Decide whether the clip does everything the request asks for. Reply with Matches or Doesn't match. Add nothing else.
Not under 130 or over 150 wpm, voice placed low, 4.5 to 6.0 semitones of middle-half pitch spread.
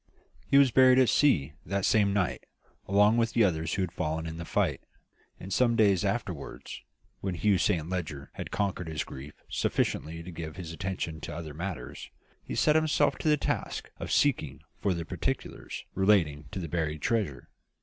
Doesn't match